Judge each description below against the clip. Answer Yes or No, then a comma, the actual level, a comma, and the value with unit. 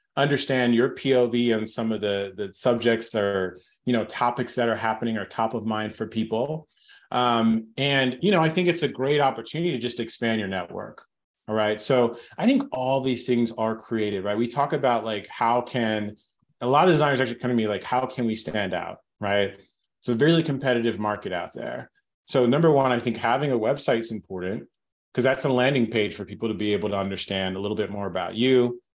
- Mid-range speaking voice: No, low, 115 Hz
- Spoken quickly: Yes, fast, 215 wpm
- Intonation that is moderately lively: Yes, average, 3.3 semitones